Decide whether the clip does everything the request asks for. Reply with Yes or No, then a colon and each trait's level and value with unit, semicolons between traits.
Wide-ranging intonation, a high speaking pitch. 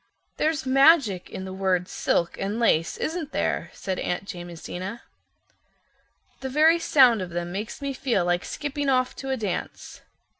Yes: wide, 7.1 semitones; high, 225 Hz